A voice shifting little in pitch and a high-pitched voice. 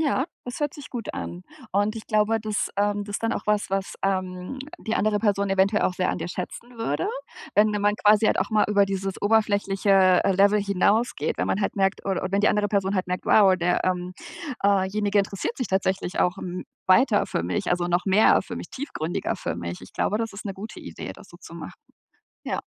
Yes: narrow, 2.2 semitones; high, 200 Hz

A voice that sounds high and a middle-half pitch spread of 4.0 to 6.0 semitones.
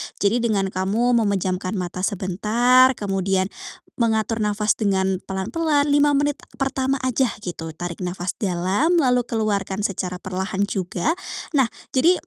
Yes: high, 205 Hz; average, 4.8 semitones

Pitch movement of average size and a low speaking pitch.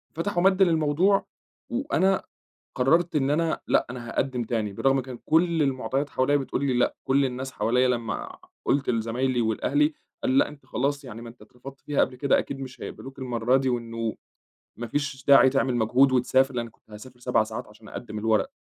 Yes: average, 3.2 semitones; low, 130 Hz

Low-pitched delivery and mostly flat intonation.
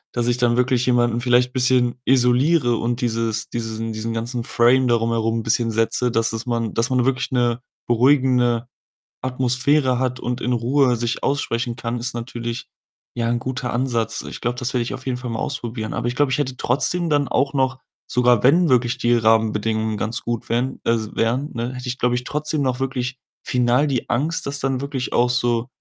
Yes: low, 125 Hz; narrow, 1.8 semitones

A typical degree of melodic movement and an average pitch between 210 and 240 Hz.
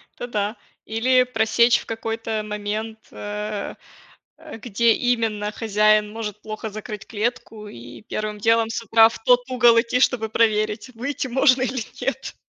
No: narrow, 2.0 semitones; high, 225 Hz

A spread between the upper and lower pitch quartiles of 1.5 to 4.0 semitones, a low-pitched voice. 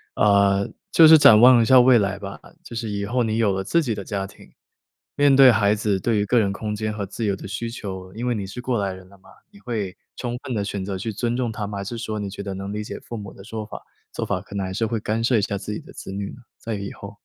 Yes: average, 2.9 semitones; low, 105 Hz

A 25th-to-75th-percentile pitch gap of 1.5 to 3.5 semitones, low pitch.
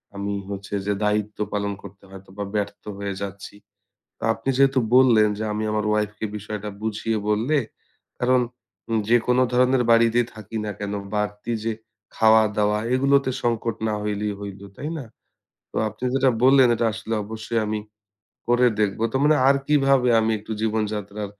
Yes: average, 2.9 semitones; low, 110 Hz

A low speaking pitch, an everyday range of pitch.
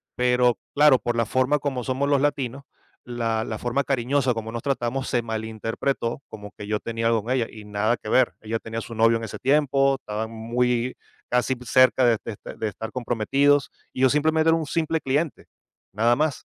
Yes: low, 125 Hz; average, 3.3 semitones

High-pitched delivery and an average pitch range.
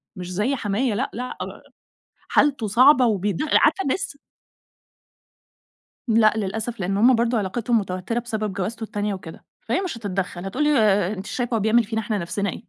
Yes: high, 220 Hz; average, 3.5 semitones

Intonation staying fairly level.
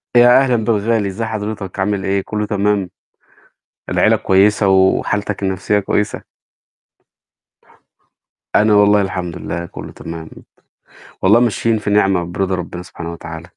Yes: narrow, 2.1 semitones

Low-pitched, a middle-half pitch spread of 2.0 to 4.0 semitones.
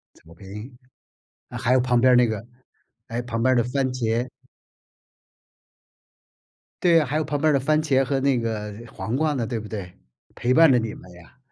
Yes: low, 125 Hz; average, 3.3 semitones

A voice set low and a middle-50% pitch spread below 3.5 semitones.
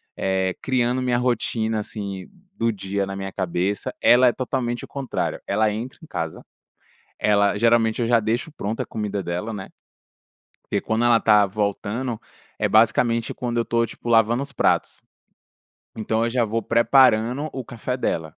Yes: low, 115 Hz; average, 2.8 semitones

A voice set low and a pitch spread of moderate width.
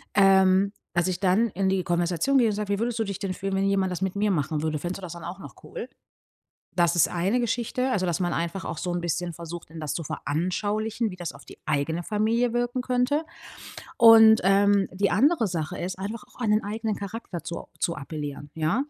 No: high, 195 Hz; average, 4.1 semitones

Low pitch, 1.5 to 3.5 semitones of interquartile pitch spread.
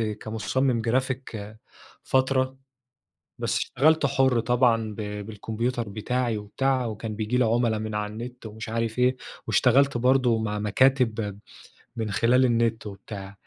Yes: low, 115 Hz; average, 2.9 semitones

